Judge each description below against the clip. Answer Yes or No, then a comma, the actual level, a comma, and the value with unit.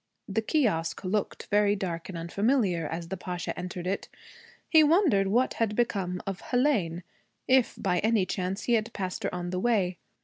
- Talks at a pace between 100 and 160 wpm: No, average, 175 wpm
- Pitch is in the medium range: No, high, 195 Hz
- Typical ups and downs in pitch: Yes, average, 4.2 semitones